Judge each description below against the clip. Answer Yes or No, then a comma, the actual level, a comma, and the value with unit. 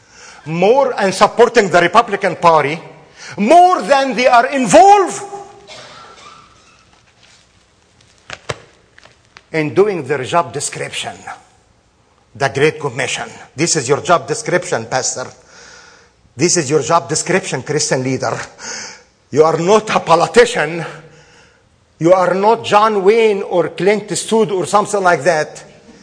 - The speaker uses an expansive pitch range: Yes, wide, 6.1 semitones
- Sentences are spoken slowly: Yes, slow, 115 wpm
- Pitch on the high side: No, medium, 175 Hz